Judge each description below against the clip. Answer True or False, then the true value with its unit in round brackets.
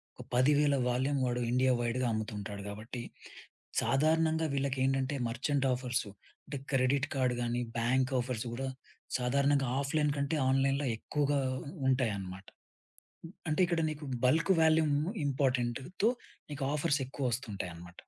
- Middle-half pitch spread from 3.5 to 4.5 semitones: False (2.9 semitones)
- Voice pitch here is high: False (135 Hz)